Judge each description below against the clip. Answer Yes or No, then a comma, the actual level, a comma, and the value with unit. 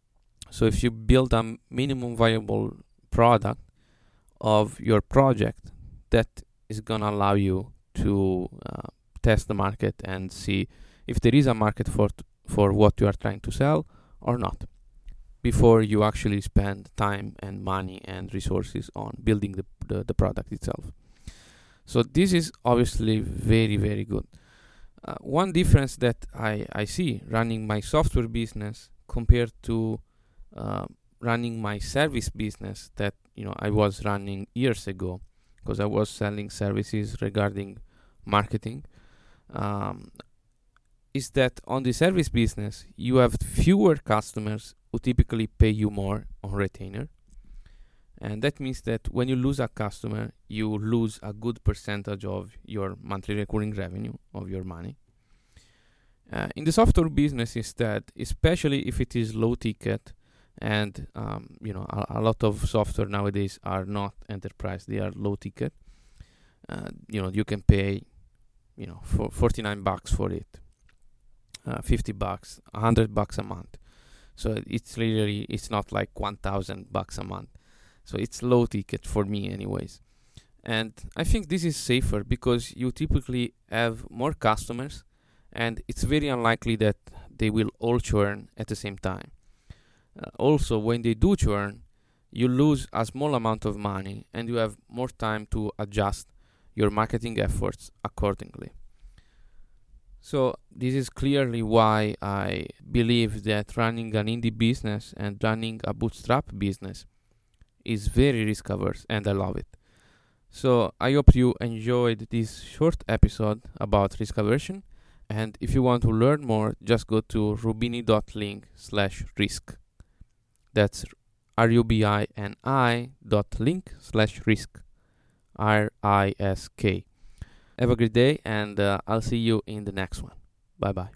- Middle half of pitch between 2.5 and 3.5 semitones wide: Yes, average, 2.8 semitones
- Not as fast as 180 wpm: Yes, average, 145 wpm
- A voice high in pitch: No, low, 110 Hz